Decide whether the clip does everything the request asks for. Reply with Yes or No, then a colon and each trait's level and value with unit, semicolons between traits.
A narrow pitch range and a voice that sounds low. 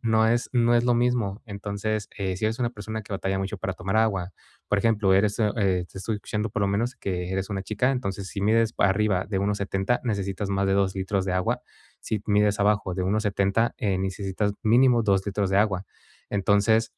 Yes: narrow, 2.3 semitones; low, 100 Hz